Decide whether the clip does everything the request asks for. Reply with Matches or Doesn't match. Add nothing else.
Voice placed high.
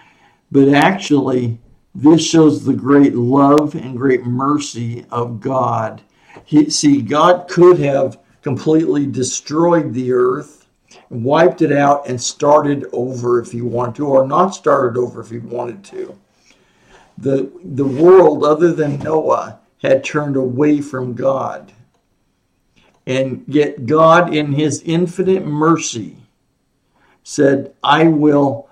Doesn't match